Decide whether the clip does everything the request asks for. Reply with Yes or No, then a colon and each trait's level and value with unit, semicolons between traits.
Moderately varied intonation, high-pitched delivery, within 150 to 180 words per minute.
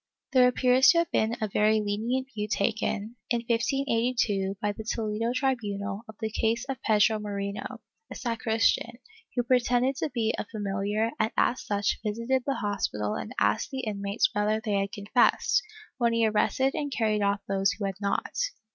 Yes: average, 3.1 semitones; high, 220 Hz; average, 175 wpm